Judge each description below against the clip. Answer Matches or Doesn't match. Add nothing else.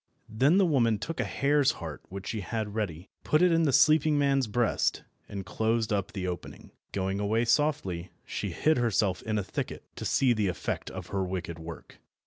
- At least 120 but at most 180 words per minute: Doesn't match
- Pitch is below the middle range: Matches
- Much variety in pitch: Matches